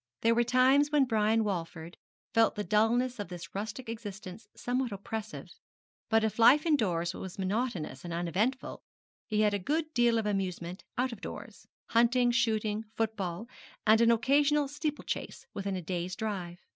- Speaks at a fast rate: No, average, 160 wpm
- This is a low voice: No, high, 220 Hz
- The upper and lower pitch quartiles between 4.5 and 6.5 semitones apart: No, average, 4.0 semitones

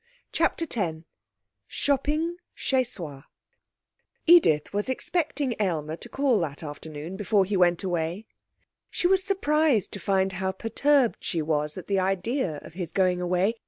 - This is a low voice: No, high, 195 Hz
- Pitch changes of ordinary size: No, wide, 7.9 semitones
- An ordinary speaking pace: Yes, average, 145 wpm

